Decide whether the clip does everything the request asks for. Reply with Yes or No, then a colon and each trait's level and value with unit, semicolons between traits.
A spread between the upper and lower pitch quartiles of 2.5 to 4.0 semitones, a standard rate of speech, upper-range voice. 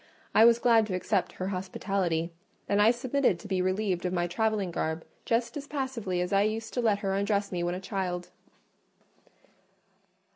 Yes: average, 3.6 semitones; average, 180 wpm; high, 200 Hz